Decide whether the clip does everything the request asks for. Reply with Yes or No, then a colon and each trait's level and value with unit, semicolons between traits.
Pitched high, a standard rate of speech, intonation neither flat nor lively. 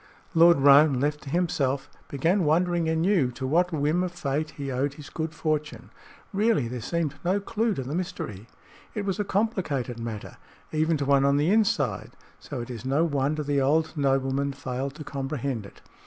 No: medium, 145 Hz; average, 185 wpm; average, 3.9 semitones